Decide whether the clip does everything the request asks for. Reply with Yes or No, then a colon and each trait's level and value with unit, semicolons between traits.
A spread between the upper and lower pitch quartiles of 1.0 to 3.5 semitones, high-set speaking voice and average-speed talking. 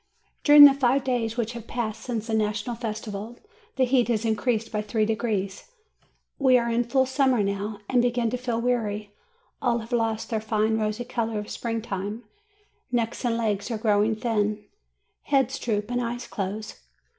Yes: narrow, 2.4 semitones; high, 230 Hz; average, 175 wpm